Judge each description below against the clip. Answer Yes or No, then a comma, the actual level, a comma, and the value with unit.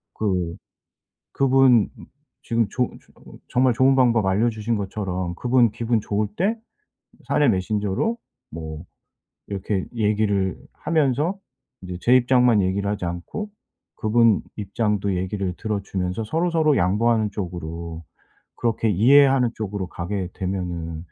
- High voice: No, low, 105 Hz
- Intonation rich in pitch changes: No, average, 4.6 semitones